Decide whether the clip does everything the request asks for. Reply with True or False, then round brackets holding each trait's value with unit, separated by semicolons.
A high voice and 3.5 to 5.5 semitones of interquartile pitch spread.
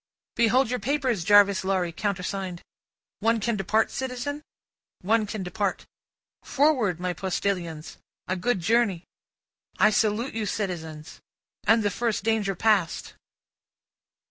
True (205 Hz; 3.8 semitones)